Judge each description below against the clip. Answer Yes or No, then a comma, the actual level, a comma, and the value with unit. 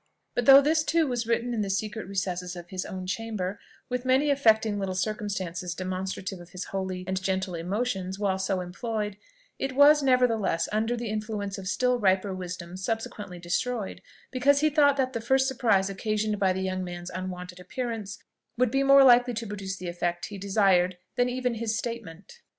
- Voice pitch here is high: Yes, high, 205 Hz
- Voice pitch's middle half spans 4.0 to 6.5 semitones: Yes, average, 4.7 semitones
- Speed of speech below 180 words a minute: No, average, 185 wpm